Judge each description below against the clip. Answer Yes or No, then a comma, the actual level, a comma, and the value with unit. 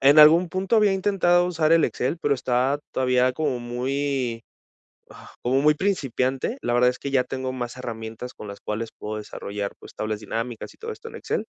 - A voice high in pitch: No, low, 130 Hz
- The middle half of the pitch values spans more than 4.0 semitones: Yes, average, 4.7 semitones